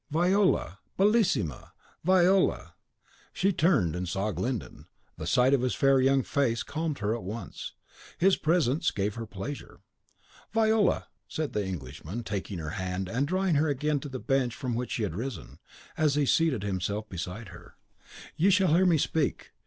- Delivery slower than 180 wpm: Yes, average, 165 wpm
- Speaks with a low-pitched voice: Yes, low, 130 Hz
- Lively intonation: Yes, wide, 8.2 semitones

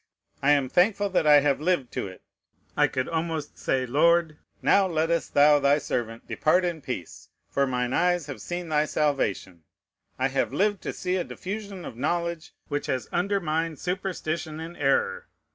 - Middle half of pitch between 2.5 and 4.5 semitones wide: Yes, average, 4.2 semitones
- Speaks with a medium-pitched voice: Yes, medium, 155 Hz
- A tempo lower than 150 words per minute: No, average, 170 wpm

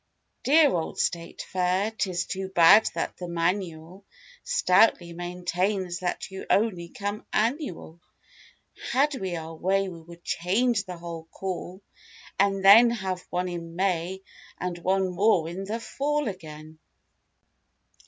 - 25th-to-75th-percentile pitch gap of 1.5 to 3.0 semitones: Yes, average, 2.7 semitones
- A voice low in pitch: No, medium, 185 Hz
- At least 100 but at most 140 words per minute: Yes, slow, 135 wpm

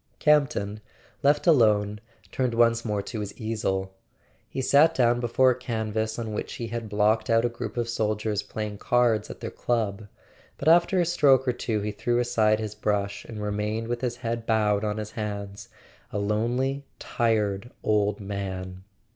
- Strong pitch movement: No, narrow, 2.5 semitones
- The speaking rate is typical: Yes, average, 170 wpm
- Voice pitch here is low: Yes, low, 110 Hz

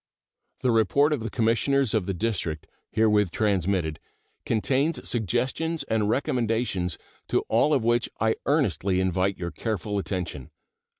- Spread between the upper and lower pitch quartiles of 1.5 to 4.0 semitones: No, average, 4.6 semitones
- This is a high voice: No, low, 110 Hz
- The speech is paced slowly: Yes, slow, 130 wpm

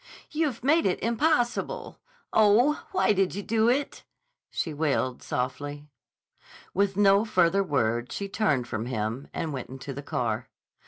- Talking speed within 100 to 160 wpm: Yes, average, 145 wpm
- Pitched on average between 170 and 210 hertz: Yes, medium, 185 Hz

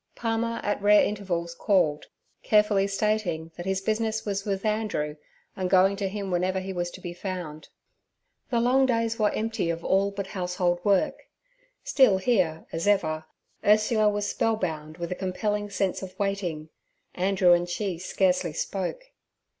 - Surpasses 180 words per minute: No, average, 155 wpm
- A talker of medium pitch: No, high, 195 Hz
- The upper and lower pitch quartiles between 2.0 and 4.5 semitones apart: Yes, average, 3.2 semitones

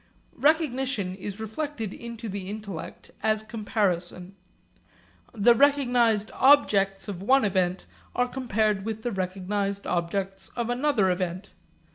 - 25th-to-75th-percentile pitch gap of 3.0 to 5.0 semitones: Yes, average, 3.9 semitones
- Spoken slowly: Yes, slow, 115 wpm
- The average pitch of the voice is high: Yes, high, 210 Hz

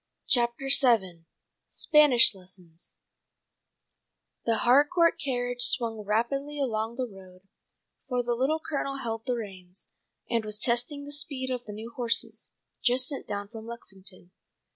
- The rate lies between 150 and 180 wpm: No, slow, 135 wpm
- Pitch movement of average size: Yes, average, 4.0 semitones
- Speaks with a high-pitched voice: Yes, high, 235 Hz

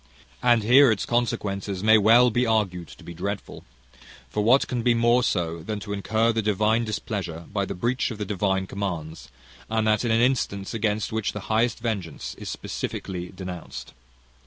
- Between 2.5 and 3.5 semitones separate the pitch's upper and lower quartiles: Yes, average, 3.2 semitones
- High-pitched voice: No, low, 105 Hz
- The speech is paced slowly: No, average, 180 wpm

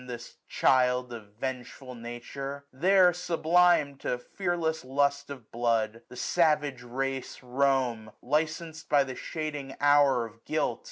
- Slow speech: Yes, slow, 125 wpm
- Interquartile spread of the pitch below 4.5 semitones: Yes, average, 3.9 semitones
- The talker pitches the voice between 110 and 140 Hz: Yes, low, 135 Hz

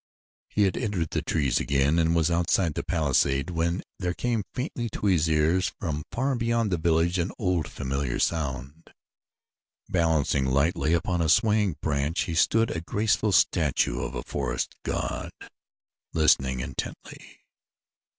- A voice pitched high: No, very low, 85 Hz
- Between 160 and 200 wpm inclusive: No, average, 145 wpm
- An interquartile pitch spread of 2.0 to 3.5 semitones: No, average, 4.1 semitones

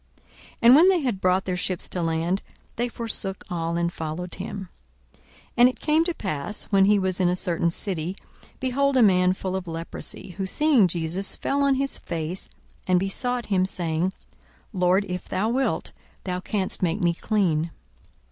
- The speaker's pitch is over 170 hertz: Yes, high, 190 Hz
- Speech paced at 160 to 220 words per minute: Yes, average, 180 wpm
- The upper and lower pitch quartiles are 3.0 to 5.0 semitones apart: Yes, average, 4.3 semitones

